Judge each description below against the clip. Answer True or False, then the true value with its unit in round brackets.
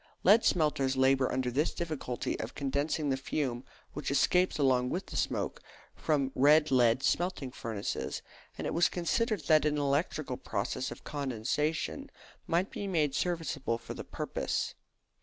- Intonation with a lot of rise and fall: False (3.8 semitones)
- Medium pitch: True (145 Hz)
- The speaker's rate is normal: True (150 wpm)